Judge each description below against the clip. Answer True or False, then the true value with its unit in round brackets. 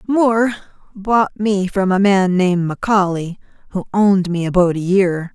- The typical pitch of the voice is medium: False (195 Hz)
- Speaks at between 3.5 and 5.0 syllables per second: True (4.8 syllables/s)